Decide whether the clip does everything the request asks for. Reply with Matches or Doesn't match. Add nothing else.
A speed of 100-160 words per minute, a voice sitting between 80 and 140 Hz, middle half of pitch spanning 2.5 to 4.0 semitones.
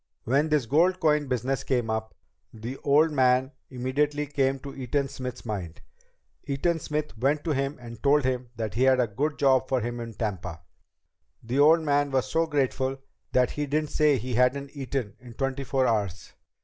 Doesn't match